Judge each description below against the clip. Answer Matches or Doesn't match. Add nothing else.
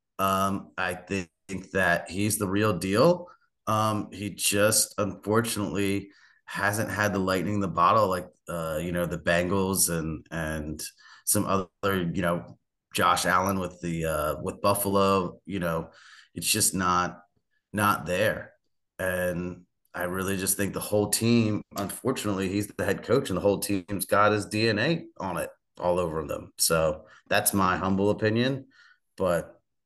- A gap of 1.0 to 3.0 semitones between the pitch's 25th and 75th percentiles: Matches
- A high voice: Doesn't match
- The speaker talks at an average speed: Matches